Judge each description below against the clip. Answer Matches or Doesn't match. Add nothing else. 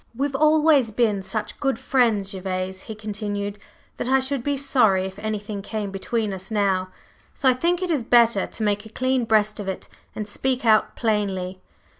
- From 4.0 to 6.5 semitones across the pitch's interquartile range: Matches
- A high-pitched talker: Matches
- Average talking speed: Matches